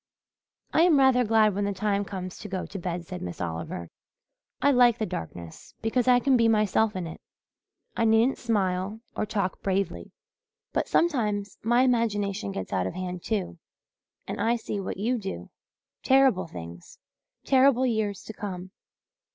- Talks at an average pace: Yes, average, 165 wpm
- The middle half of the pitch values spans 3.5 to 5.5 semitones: Yes, average, 4.3 semitones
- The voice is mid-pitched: No, high, 205 Hz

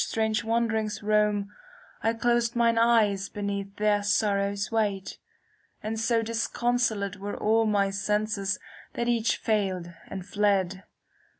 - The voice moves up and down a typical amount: No, narrow, 2.2 semitones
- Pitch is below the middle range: No, high, 210 Hz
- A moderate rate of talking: No, slow, 115 wpm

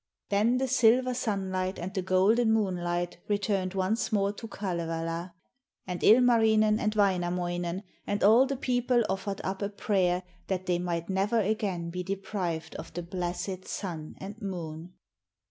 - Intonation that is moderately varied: Yes, average, 3.4 semitones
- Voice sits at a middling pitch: No, high, 195 Hz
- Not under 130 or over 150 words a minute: Yes, average, 145 wpm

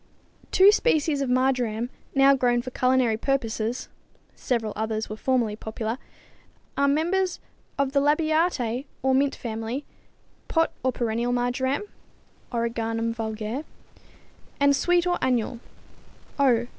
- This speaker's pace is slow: Yes, slow, 125 wpm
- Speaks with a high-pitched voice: Yes, very high, 255 Hz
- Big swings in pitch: No, average, 3.6 semitones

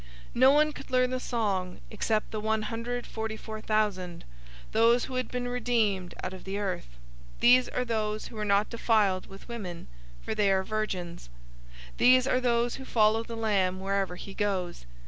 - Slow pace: No, average, 185 wpm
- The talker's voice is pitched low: No, high, 215 Hz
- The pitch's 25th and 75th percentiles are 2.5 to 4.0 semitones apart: Yes, average, 3.6 semitones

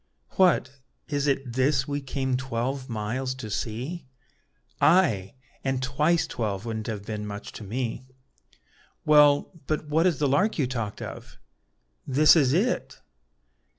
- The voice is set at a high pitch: No, low, 130 Hz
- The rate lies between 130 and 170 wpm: Yes, average, 140 wpm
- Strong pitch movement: No, average, 4.4 semitones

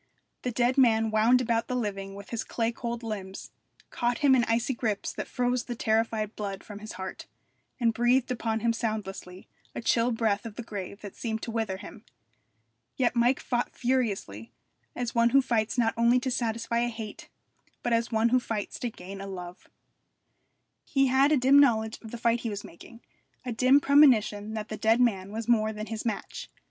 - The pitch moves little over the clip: Yes, narrow, 2.3 semitones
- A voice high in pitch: Yes, high, 230 Hz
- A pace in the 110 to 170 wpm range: No, average, 195 wpm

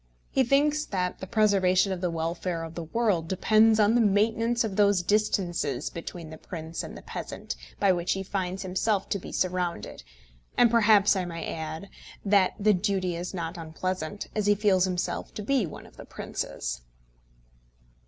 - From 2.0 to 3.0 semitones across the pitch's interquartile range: No, average, 3.4 semitones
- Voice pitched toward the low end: No, high, 190 Hz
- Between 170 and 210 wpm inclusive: Yes, average, 175 wpm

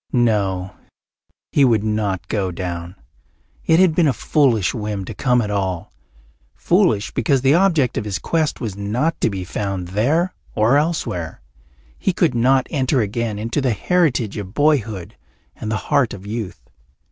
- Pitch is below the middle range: Yes, low, 110 Hz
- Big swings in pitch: Yes, wide, 6.2 semitones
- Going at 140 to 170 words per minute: Yes, average, 160 wpm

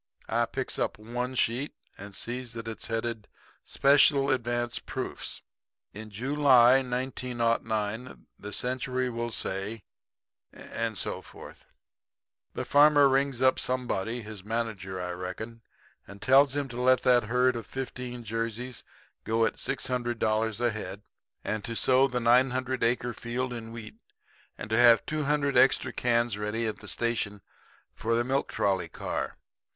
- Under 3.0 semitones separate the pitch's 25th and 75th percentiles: Yes, narrow, 2.5 semitones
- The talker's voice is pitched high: No, low, 120 Hz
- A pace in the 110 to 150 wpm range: Yes, average, 145 wpm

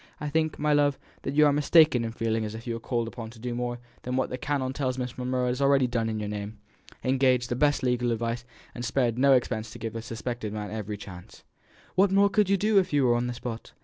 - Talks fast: Yes, fast, 260 wpm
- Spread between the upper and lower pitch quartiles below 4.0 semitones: Yes, average, 3.4 semitones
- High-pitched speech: No, low, 125 Hz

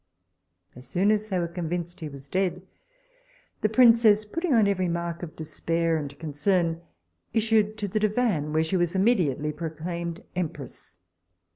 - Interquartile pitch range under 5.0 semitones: Yes, average, 4.6 semitones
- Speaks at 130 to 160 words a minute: Yes, average, 150 wpm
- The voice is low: No, medium, 175 Hz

